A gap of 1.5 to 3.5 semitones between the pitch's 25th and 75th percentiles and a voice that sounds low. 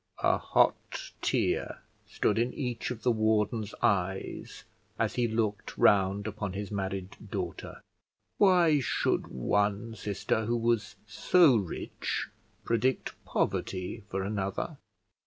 Yes: average, 3.0 semitones; low, 105 Hz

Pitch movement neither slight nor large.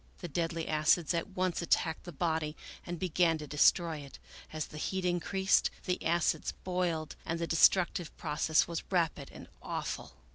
No: narrow, 2.2 semitones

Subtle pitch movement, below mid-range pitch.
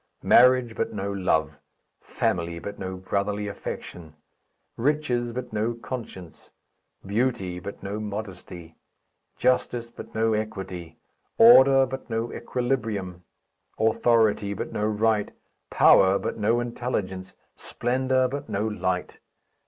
No: average, 4.2 semitones; low, 110 Hz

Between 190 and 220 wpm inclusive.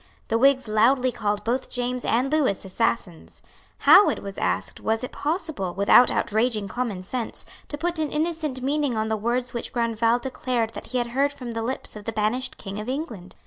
Yes: average, 195 wpm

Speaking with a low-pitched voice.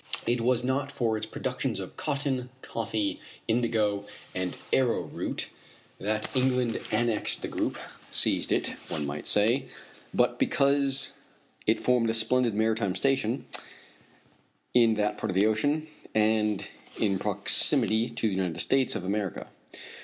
Yes: low, 115 Hz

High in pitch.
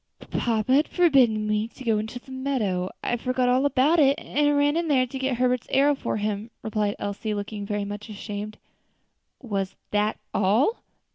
Yes: high, 230 Hz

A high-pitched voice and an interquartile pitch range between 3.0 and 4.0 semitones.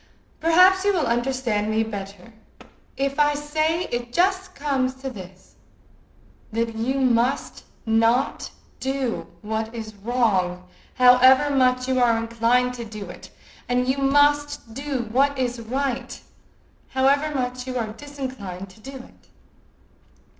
Yes: very high, 250 Hz; average, 3.5 semitones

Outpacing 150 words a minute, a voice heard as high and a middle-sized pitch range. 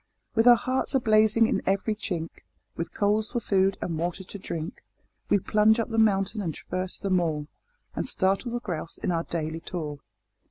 Yes: average, 190 wpm; high, 195 Hz; average, 4.4 semitones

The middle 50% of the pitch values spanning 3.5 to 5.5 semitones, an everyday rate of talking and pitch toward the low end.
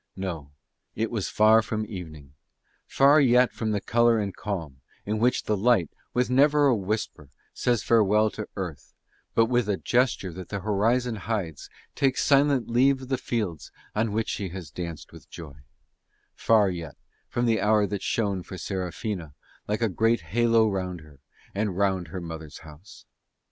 Yes: average, 4.4 semitones; average, 170 wpm; low, 105 Hz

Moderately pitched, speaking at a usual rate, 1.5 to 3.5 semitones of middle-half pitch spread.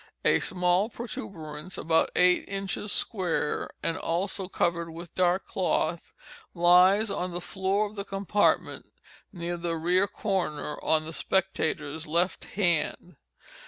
No: medium, 180 Hz; slow, 125 wpm; average, 2.8 semitones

